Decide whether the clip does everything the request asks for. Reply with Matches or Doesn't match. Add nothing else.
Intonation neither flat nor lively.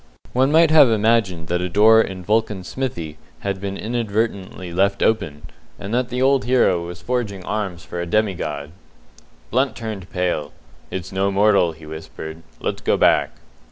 Matches